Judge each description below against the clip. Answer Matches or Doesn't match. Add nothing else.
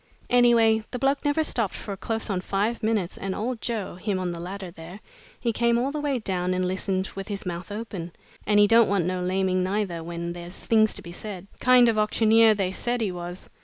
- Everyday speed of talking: Doesn't match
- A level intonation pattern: Doesn't match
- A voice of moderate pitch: Doesn't match